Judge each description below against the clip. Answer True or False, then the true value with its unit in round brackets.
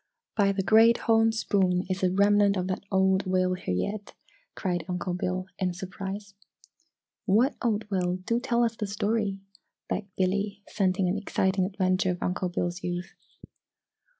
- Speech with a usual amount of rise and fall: False (2.1 semitones)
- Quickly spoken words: False (155 wpm)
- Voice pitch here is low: False (190 Hz)